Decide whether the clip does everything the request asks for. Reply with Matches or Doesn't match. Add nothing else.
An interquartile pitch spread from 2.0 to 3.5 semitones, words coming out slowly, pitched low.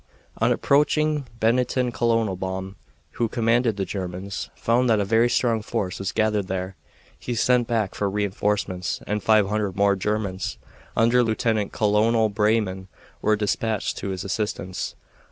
Doesn't match